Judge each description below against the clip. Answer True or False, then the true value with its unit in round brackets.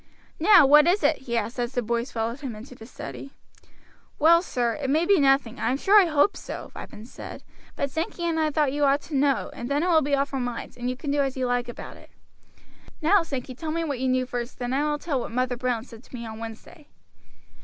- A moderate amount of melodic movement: True (3.6 semitones)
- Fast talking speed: True (250 wpm)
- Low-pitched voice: False (270 Hz)